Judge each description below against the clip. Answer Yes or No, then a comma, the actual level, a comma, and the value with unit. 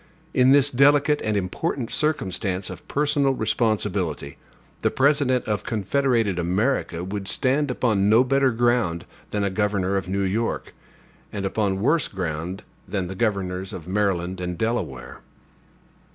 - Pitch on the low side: Yes, low, 105 Hz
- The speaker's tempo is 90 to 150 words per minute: Yes, average, 140 wpm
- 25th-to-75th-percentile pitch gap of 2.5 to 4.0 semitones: No, wide, 5.4 semitones